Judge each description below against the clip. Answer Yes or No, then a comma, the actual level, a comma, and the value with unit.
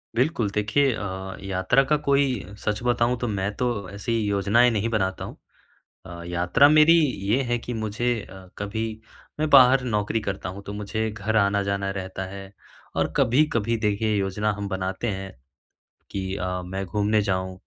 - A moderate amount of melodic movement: Yes, average, 3.4 semitones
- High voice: No, low, 105 Hz